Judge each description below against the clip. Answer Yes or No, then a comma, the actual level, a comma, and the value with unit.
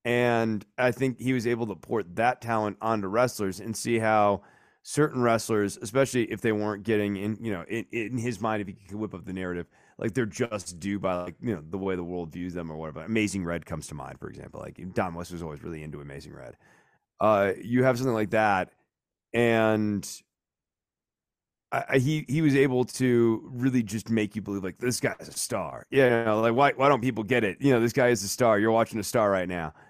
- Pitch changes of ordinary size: Yes, average, 4.0 semitones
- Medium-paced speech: No, fast, 235 wpm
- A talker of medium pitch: No, low, 110 Hz